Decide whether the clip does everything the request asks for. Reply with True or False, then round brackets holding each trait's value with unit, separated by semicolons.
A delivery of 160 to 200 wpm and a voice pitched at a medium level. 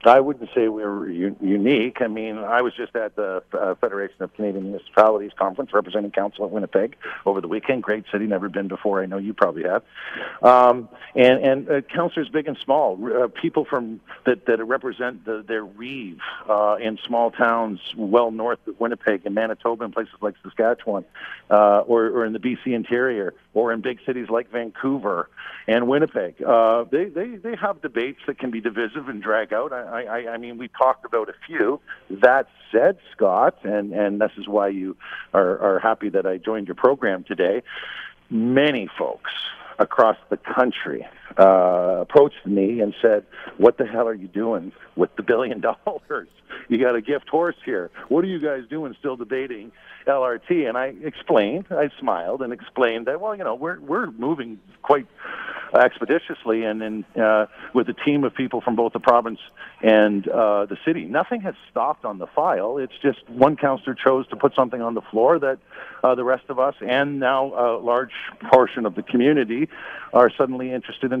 False (190 wpm; 115 Hz)